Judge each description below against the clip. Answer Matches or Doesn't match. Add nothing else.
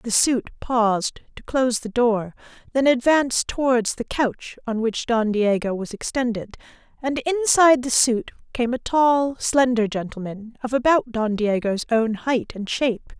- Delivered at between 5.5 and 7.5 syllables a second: Doesn't match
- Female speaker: Matches